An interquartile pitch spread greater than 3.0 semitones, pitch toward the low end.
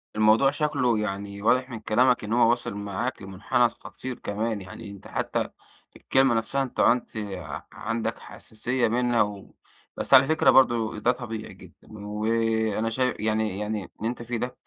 No: average, 2.7 semitones; low, 115 Hz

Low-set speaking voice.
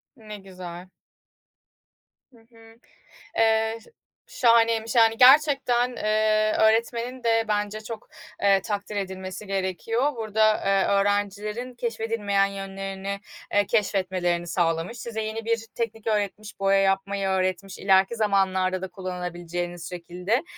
No: high, 205 Hz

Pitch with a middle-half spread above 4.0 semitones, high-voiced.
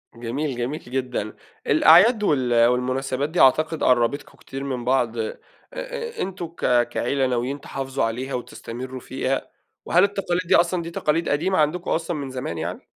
No: average, 5.2 semitones; low, 135 Hz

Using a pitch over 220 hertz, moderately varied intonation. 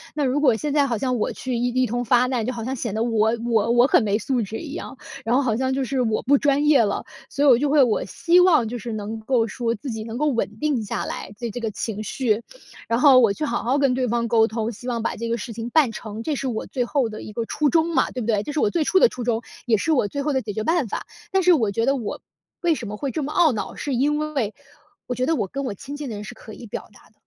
Yes: high, 245 Hz; average, 3.9 semitones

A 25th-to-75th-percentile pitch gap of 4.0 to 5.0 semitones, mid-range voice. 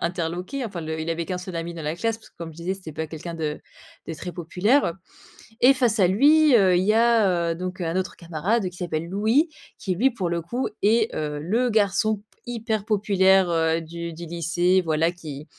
Yes: average, 4.5 semitones; medium, 180 Hz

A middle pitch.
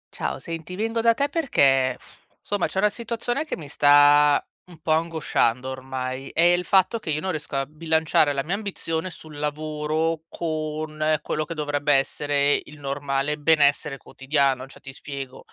Yes: medium, 150 Hz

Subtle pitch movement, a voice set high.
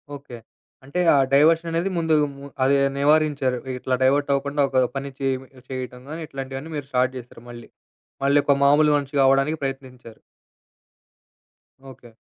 No: narrow, 2.1 semitones; medium, 140 Hz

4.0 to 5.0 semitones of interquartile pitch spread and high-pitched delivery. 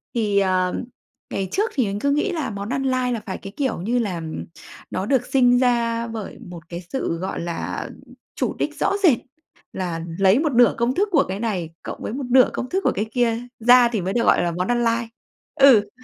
Yes: average, 4.7 semitones; high, 230 Hz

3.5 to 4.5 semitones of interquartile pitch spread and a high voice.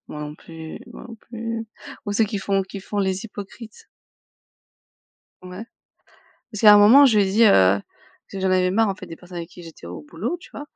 Yes: average, 3.9 semitones; high, 195 Hz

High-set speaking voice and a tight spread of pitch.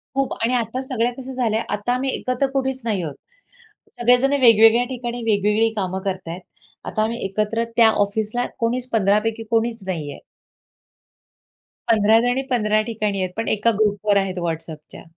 No: high, 225 Hz; average, 3.0 semitones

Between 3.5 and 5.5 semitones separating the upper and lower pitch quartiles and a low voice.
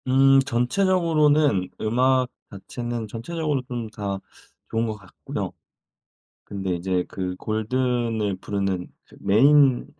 Yes: average, 5.1 semitones; low, 120 Hz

